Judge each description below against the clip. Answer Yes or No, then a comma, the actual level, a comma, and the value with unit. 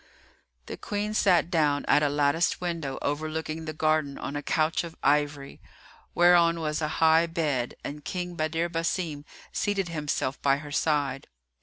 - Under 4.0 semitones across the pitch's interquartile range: Yes, narrow, 2.4 semitones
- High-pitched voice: No, medium, 155 Hz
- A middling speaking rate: Yes, average, 155 wpm